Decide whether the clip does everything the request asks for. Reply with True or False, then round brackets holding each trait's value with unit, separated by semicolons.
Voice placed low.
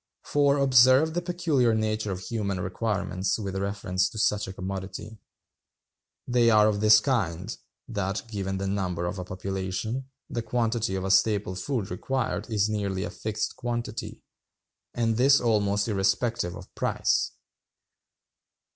True (105 Hz)